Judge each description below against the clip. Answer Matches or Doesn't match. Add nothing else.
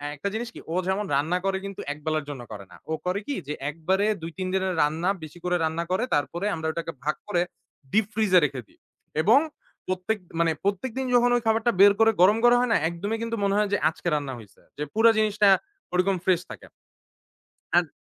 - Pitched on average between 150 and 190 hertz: Matches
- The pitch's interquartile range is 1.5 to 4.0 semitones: Doesn't match